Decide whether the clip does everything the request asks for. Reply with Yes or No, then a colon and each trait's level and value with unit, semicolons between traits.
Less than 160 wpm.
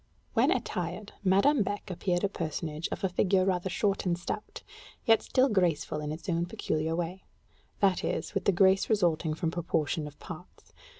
No: average, 175 wpm